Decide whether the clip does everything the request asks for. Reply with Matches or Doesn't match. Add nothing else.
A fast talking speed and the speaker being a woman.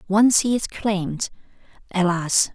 Doesn't match